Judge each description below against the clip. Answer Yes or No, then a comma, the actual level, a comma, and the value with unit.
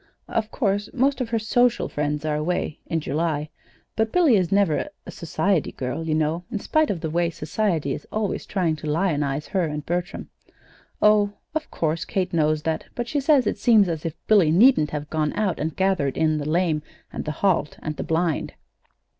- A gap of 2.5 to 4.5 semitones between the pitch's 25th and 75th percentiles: No, average, 5.2 semitones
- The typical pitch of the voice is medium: Yes, medium, 170 Hz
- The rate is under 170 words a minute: No, average, 195 wpm